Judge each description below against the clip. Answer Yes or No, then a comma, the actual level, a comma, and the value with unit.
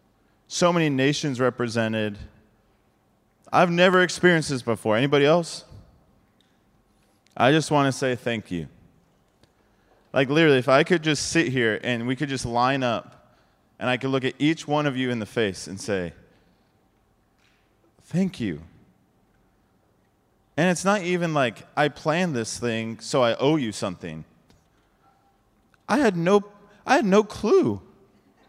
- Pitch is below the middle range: Yes, low, 125 Hz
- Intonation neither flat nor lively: No, wide, 6.6 semitones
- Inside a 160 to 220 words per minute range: No, average, 145 wpm